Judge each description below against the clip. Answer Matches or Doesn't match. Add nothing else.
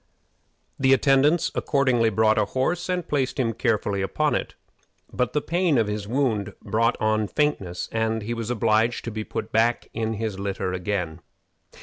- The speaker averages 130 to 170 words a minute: Matches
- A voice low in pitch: Matches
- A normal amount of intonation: Matches